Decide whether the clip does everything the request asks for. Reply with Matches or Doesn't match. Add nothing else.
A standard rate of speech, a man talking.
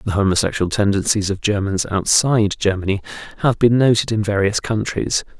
Matches